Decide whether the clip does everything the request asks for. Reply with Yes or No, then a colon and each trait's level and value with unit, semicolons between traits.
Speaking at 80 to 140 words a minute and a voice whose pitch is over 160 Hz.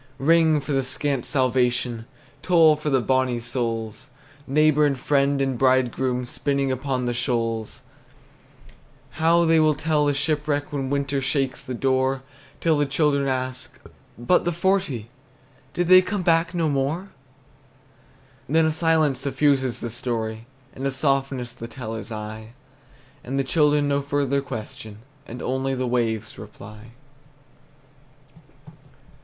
No: slow, 135 wpm; low, 135 Hz